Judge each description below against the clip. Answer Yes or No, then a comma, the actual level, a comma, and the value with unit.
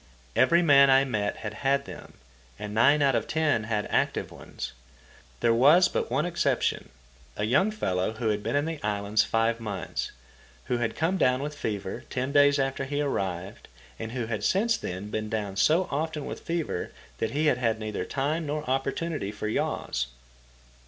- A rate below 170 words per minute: No, average, 180 wpm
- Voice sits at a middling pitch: No, low, 130 Hz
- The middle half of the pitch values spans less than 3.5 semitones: No, wide, 5.5 semitones